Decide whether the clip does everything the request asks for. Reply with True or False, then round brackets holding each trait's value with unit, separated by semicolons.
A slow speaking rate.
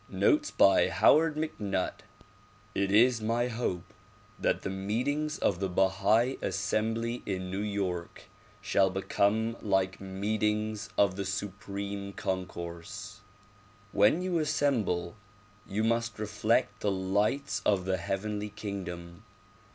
True (115 wpm)